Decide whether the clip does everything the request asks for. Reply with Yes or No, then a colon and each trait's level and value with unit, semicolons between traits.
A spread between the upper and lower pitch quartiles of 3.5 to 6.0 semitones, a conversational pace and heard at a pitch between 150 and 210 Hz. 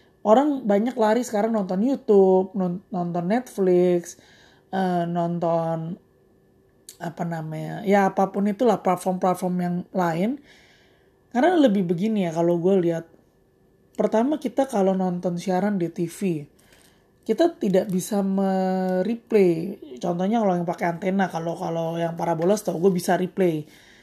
No: average, 2.8 semitones; average, 120 wpm; medium, 185 Hz